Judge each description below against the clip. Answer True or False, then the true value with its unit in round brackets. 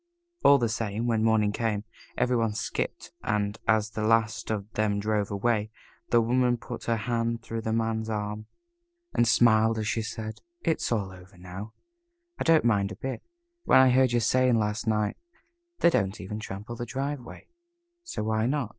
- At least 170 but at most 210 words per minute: True (175 wpm)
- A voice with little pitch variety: True (2.2 semitones)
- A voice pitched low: True (110 Hz)